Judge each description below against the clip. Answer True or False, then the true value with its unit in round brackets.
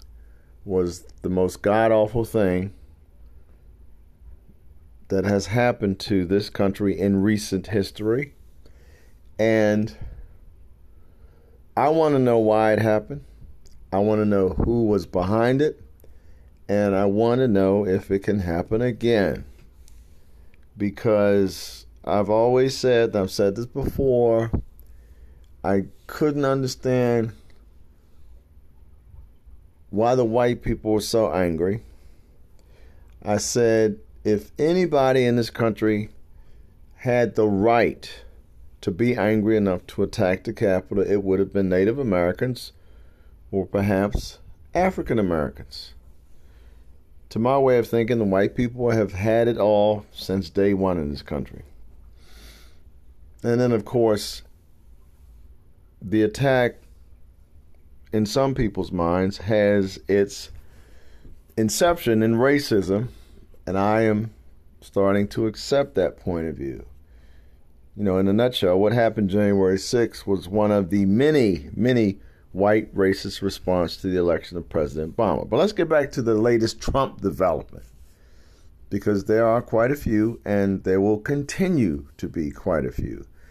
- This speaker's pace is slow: True (130 wpm)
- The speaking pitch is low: True (95 Hz)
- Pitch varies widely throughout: True (6.0 semitones)